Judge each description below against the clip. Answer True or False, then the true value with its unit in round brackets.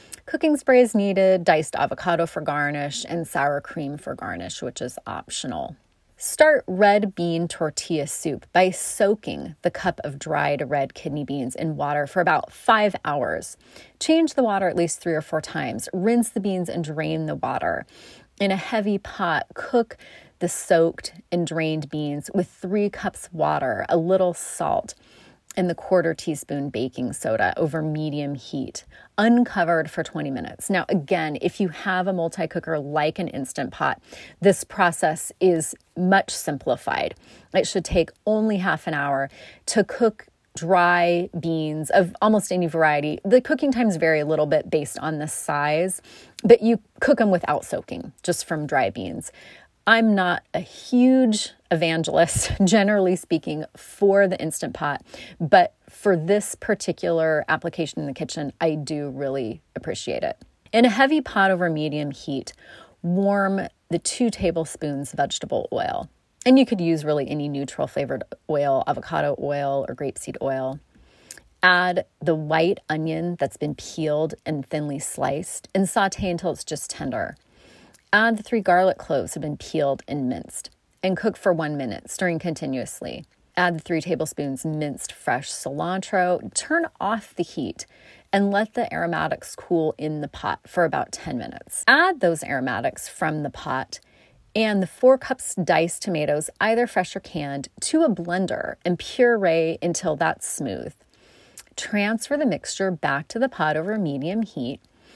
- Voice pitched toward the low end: False (175 Hz)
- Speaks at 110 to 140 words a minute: False (155 wpm)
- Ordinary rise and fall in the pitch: True (4.5 semitones)